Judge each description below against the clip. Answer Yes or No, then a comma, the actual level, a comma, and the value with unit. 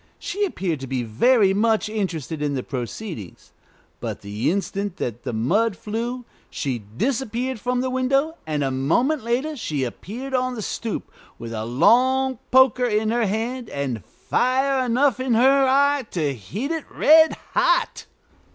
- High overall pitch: Yes, high, 225 Hz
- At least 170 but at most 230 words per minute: No, average, 160 wpm